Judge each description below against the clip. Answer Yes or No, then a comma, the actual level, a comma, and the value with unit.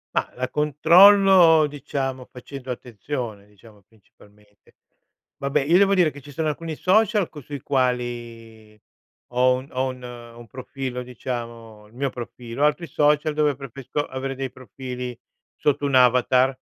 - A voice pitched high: No, low, 130 Hz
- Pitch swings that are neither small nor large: Yes, average, 3.7 semitones